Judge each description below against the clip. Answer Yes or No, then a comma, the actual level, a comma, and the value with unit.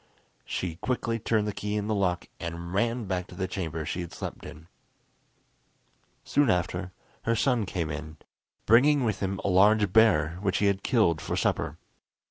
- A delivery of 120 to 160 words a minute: No, average, 175 wpm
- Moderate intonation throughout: Yes, average, 4.0 semitones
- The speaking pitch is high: No, very low, 95 Hz